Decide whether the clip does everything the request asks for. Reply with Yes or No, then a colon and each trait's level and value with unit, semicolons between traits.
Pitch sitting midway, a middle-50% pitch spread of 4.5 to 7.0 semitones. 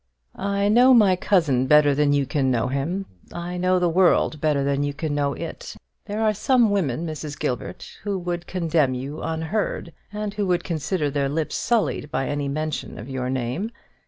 Yes: medium, 155 Hz; average, 5.0 semitones